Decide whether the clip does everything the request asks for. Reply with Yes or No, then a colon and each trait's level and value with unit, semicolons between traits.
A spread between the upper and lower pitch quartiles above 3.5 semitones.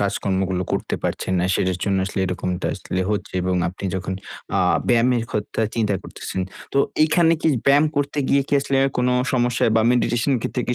Yes: average, 5.2 semitones